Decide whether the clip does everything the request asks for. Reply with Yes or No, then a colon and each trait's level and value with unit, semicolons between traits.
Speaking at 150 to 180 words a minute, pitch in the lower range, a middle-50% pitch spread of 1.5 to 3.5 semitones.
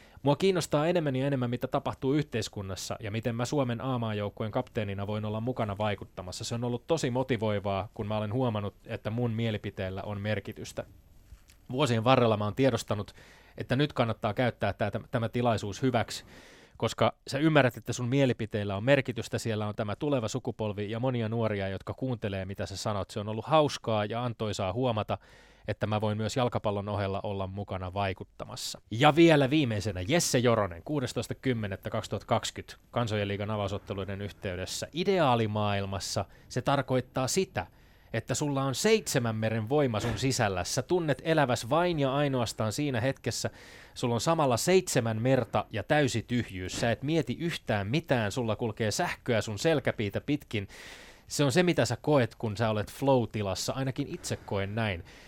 No: fast, 155 wpm; low, 115 Hz; average, 4.1 semitones